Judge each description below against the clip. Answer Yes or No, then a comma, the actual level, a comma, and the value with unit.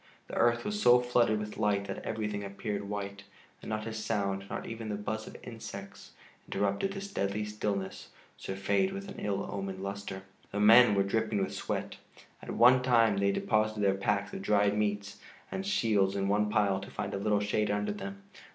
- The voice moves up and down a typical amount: No, narrow, 1.9 semitones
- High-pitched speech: No, low, 105 Hz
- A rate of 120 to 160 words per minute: No, average, 190 wpm